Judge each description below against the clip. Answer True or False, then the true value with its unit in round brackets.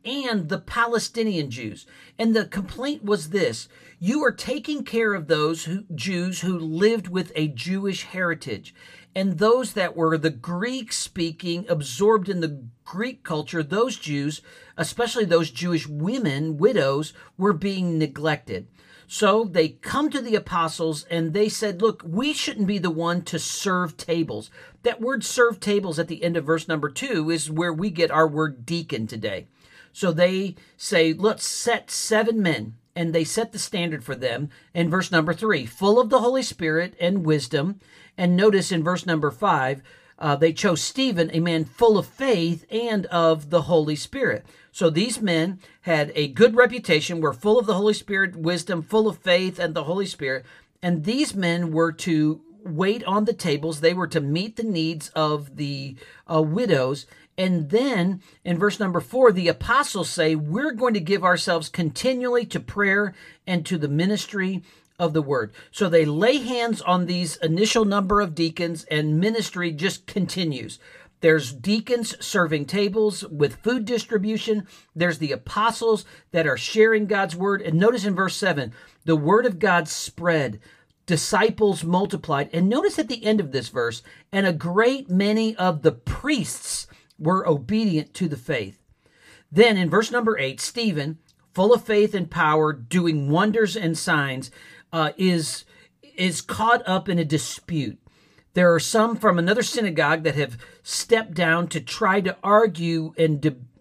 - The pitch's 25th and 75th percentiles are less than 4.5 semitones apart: False (4.8 semitones)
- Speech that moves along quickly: False (170 wpm)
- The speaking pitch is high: False (175 Hz)